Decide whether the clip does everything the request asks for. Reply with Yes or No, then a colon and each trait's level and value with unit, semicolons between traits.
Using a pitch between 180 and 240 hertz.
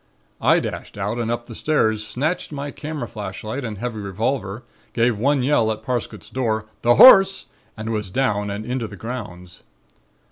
No: low, 115 Hz